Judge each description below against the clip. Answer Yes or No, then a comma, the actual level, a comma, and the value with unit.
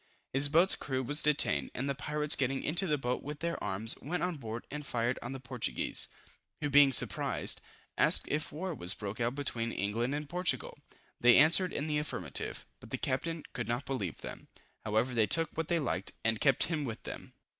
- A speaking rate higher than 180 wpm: Yes, average, 200 wpm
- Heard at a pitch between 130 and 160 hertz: Yes, low, 135 Hz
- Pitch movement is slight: No, average, 4.3 semitones